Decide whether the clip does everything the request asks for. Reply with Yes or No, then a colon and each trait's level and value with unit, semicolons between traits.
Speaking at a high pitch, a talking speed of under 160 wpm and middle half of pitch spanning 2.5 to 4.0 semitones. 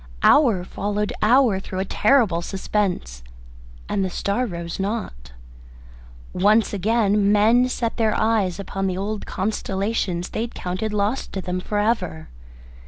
Yes: high, 205 Hz; average, 140 wpm; average, 2.9 semitones